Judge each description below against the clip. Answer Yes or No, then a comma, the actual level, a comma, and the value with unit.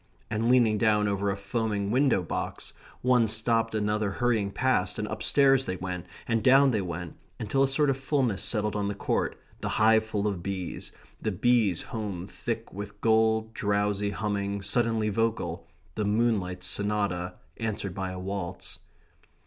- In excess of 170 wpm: No, average, 160 wpm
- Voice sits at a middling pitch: No, low, 105 Hz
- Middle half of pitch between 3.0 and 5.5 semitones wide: No, narrow, 2.5 semitones